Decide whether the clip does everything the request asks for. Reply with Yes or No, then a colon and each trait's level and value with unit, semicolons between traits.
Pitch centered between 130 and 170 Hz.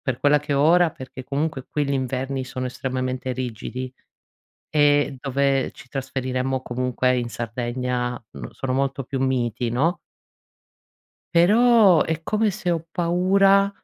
Yes: low, 135 Hz